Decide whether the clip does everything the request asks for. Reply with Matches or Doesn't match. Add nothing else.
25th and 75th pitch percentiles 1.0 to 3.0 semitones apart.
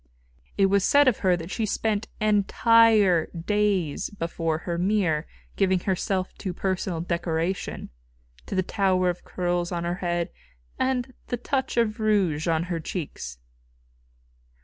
Doesn't match